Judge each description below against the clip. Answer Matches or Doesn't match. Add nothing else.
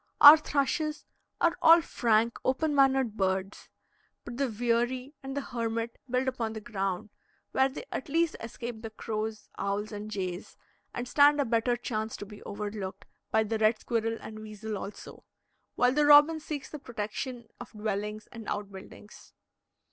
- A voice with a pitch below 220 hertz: Doesn't match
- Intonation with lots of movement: Doesn't match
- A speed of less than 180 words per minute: Matches